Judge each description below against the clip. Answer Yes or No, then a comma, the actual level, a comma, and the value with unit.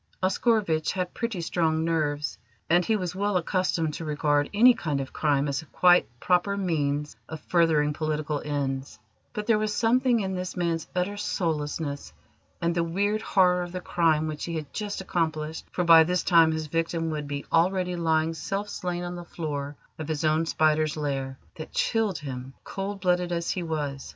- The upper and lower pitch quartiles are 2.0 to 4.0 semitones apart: Yes, average, 3.1 semitones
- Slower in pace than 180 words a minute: No, average, 185 wpm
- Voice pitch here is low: No, medium, 165 Hz